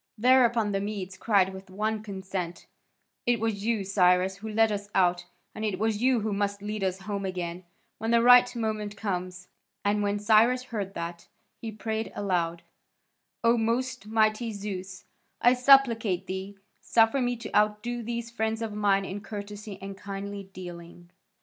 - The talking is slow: No, average, 160 wpm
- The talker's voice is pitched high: Yes, high, 205 Hz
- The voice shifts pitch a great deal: No, average, 2.7 semitones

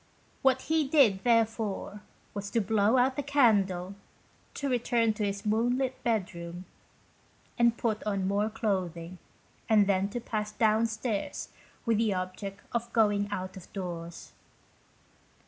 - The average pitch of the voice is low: No, high, 215 Hz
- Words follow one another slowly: Yes, slow, 130 wpm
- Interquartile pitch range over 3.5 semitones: No, average, 3.2 semitones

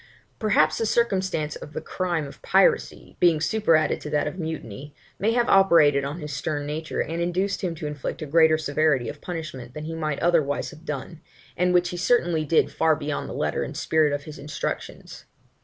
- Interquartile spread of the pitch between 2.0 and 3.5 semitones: Yes, average, 2.9 semitones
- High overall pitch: No, medium, 155 Hz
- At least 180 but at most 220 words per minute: Yes, average, 195 wpm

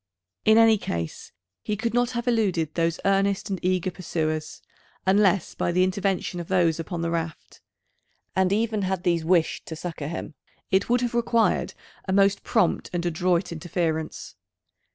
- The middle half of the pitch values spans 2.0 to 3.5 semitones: Yes, average, 3.2 semitones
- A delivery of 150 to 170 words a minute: Yes, average, 160 wpm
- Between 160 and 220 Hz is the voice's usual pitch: Yes, medium, 185 Hz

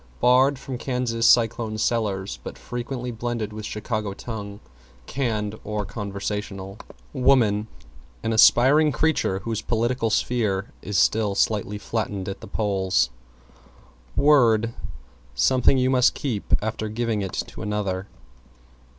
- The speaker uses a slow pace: Yes, slow, 120 wpm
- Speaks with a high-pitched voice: No, low, 110 Hz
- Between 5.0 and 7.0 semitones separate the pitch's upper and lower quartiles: No, average, 3.0 semitones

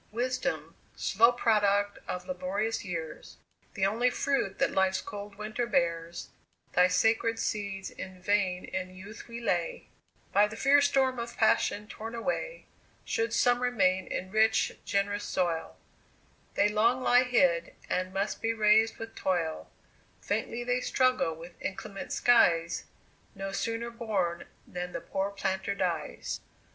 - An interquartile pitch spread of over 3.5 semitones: Yes, average, 3.9 semitones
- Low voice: No, high, 205 Hz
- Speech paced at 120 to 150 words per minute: Yes, average, 140 wpm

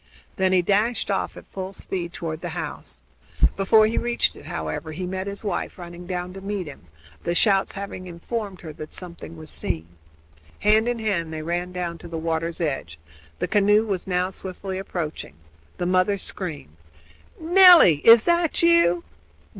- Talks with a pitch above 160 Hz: Yes, medium, 185 Hz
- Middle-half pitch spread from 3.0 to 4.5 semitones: Yes, average, 3.4 semitones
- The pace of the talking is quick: No, average, 170 wpm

